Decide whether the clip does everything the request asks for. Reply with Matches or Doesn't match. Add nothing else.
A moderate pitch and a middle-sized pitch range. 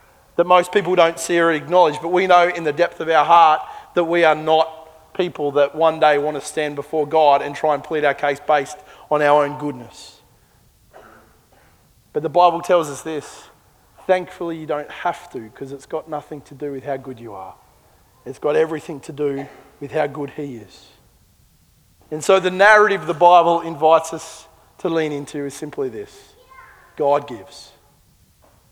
Matches